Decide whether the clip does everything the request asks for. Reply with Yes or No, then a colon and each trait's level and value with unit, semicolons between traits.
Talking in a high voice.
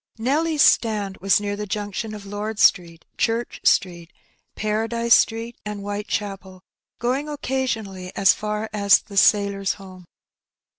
Yes: high, 210 Hz